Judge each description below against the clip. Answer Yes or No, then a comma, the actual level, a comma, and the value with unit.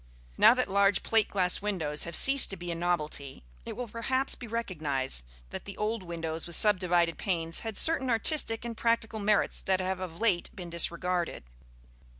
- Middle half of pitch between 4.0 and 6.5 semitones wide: Yes, average, 4.8 semitones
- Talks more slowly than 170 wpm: No, average, 175 wpm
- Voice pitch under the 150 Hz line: No, high, 190 Hz